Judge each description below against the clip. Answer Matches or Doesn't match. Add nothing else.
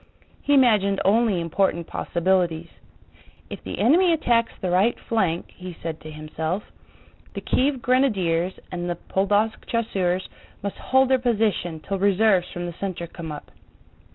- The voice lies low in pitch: Doesn't match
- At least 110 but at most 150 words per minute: Matches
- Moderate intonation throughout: Matches